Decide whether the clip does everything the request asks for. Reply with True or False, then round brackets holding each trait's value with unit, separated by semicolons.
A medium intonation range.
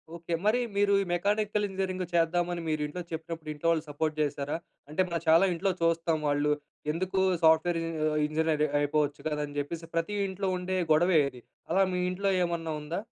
True (3.1 semitones)